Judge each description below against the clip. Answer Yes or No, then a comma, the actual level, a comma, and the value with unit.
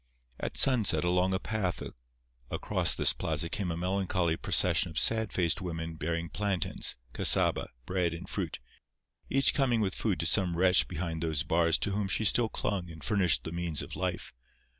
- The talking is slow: No, average, 170 wpm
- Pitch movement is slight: No, average, 3.1 semitones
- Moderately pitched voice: No, very low, 90 Hz